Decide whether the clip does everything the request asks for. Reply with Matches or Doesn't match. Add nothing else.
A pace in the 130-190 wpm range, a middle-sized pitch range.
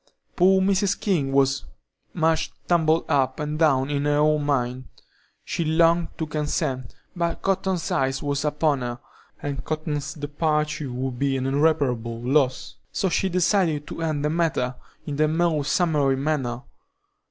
Matches